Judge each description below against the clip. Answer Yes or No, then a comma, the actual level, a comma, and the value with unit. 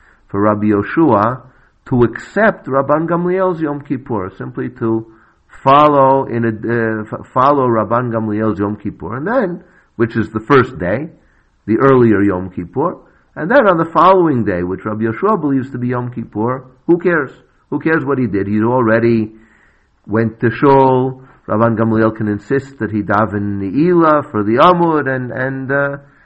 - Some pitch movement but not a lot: Yes, average, 4.6 semitones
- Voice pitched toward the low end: Yes, low, 120 Hz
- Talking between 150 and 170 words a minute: Yes, average, 165 wpm